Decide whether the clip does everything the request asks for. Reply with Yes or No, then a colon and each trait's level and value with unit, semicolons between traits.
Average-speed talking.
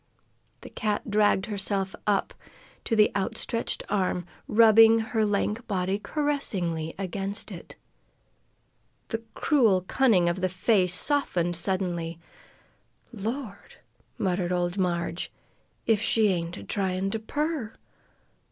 No: slow, 110 wpm